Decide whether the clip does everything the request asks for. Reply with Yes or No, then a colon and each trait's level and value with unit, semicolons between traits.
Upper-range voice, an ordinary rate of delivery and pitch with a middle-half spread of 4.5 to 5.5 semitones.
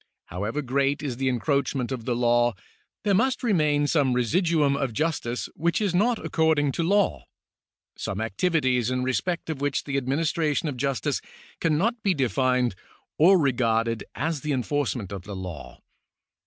No: medium, 140 Hz; average, 155 wpm; average, 4.9 semitones